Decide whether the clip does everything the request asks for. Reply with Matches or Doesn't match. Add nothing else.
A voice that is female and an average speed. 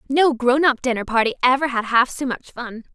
Doesn't match